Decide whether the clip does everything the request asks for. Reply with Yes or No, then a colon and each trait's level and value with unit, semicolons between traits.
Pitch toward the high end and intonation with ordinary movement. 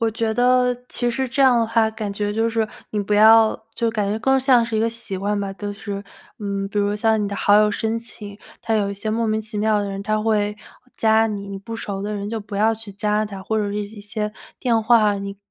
No: high, 215 Hz; narrow, 1.7 semitones